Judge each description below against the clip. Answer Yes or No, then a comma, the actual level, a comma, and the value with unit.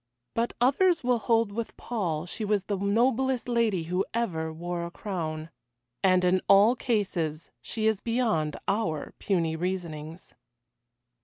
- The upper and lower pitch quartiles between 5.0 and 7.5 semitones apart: Yes, wide, 5.5 semitones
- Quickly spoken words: No, average, 140 wpm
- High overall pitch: Yes, high, 195 Hz